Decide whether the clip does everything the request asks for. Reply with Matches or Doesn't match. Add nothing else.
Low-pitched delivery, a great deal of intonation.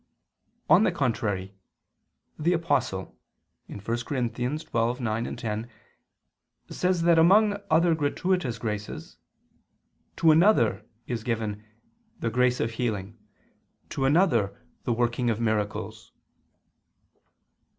Matches